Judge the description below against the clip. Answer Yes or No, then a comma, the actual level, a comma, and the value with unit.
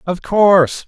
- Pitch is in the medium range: Yes, medium, 180 Hz